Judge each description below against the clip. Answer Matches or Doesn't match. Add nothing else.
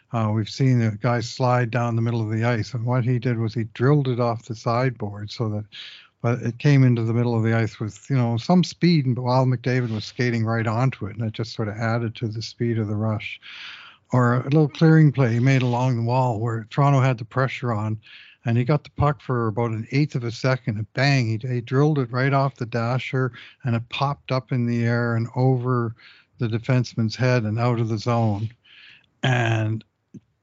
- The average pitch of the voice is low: Matches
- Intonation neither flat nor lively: Doesn't match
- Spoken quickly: Matches